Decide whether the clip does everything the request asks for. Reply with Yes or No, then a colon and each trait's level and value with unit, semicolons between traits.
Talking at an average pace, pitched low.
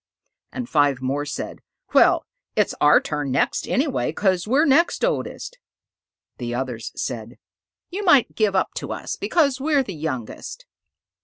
No: average, 145 wpm; high, 190 Hz